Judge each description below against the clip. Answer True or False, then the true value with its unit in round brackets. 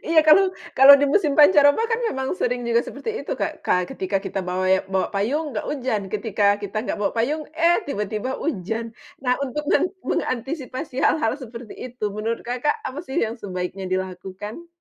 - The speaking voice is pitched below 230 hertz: False (240 Hz)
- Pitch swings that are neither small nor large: False (5.9 semitones)